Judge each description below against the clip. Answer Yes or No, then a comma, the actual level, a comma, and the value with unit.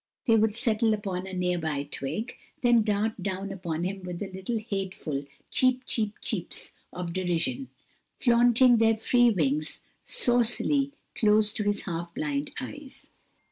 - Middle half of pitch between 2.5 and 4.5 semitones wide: No, average, 4.9 semitones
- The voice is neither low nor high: No, high, 210 Hz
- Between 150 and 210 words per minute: No, average, 140 wpm